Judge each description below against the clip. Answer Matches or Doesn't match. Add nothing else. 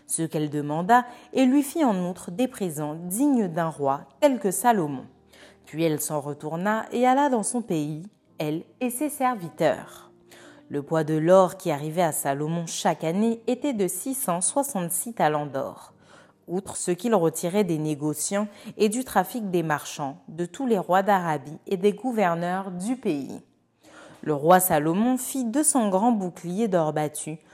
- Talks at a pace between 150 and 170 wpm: Matches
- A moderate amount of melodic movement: Doesn't match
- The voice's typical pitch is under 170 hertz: Doesn't match